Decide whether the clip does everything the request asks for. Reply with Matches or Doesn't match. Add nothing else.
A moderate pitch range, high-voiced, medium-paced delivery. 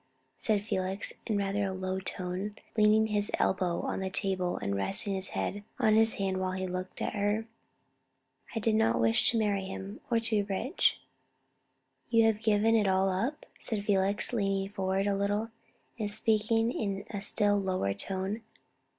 Doesn't match